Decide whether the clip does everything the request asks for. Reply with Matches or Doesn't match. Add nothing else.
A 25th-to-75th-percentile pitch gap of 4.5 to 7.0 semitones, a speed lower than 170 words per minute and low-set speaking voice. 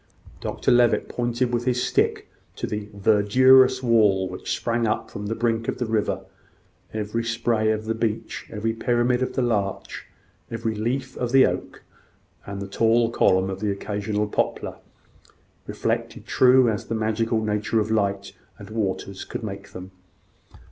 Doesn't match